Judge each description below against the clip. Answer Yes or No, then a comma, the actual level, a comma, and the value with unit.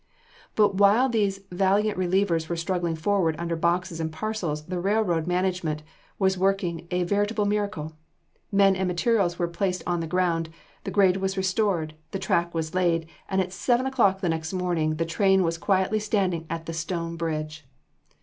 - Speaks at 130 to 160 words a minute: No, average, 170 wpm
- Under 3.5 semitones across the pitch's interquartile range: Yes, average, 2.9 semitones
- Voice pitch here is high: No, medium, 180 Hz